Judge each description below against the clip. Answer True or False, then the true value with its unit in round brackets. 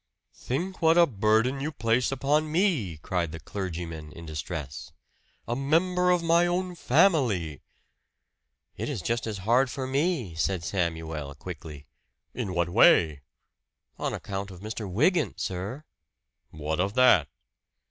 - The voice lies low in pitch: True (110 Hz)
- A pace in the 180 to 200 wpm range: False (135 wpm)